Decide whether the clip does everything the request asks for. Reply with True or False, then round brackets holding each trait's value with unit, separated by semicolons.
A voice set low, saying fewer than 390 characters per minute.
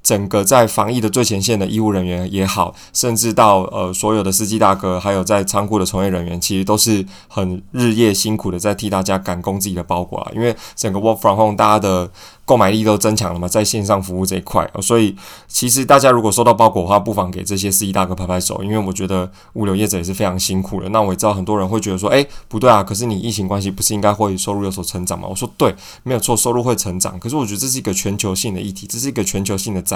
False (100 Hz; 420 characters per minute)